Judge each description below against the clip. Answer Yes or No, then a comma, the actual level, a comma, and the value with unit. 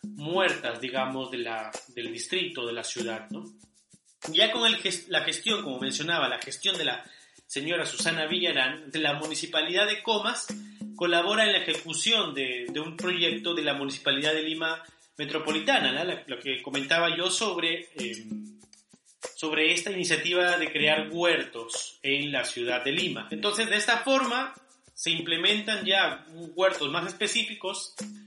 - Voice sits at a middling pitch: Yes, medium, 165 Hz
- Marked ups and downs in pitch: Yes, wide, 6.0 semitones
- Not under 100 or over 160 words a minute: Yes, average, 155 wpm